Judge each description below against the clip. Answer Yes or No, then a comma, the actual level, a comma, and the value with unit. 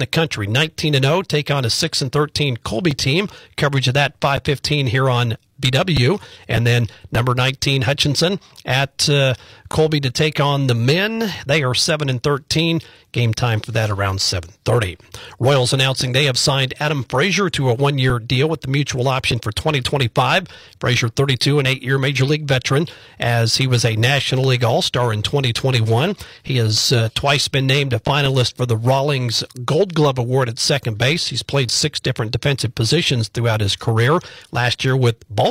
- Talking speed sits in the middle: Yes, average, 195 wpm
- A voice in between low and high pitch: No, low, 130 Hz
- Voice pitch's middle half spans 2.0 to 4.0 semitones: Yes, average, 3.1 semitones